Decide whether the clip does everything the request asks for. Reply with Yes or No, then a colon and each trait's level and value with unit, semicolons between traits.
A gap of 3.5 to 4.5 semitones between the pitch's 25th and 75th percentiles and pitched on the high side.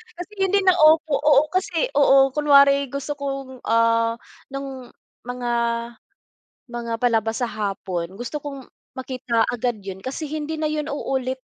Yes: average, 3.9 semitones; very high, 270 Hz